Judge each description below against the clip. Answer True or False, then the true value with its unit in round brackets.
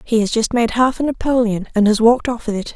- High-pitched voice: True (230 Hz)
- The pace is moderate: False (285 wpm)